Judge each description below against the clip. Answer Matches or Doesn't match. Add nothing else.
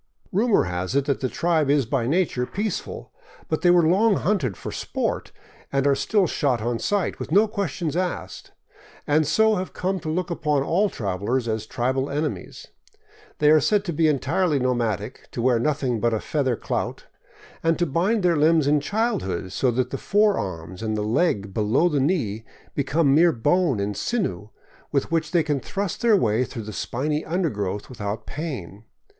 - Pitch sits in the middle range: Matches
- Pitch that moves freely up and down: Matches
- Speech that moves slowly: Doesn't match